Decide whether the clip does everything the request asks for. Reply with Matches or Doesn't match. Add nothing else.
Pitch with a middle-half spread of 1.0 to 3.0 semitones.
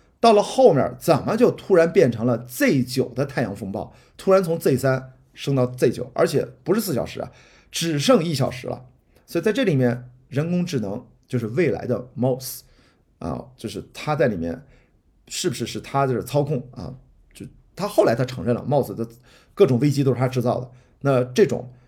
Matches